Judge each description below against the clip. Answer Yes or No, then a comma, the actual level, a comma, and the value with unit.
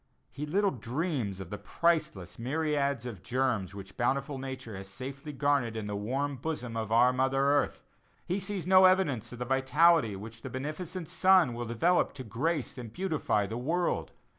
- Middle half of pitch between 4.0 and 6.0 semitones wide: Yes, wide, 5.6 semitones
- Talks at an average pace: Yes, average, 175 wpm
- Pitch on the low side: Yes, low, 130 Hz